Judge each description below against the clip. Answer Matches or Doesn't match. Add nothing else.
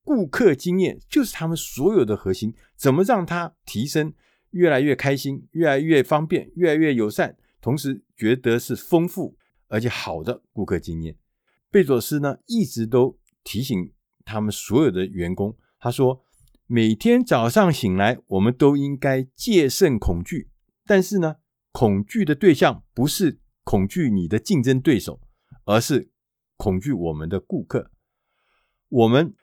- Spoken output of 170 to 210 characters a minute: Doesn't match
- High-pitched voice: Doesn't match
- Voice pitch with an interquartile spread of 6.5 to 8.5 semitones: Matches